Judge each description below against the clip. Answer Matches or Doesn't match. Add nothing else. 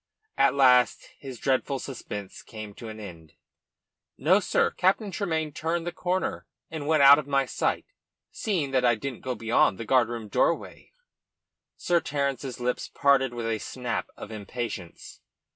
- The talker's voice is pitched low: Matches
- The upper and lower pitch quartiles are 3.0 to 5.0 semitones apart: Matches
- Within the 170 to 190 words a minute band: Doesn't match